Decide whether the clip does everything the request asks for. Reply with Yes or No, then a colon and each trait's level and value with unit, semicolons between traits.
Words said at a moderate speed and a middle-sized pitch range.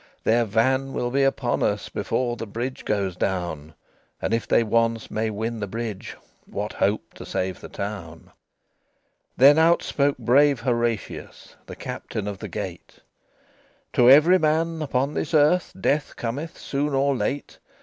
Yes: average, 160 wpm; average, 4.8 semitones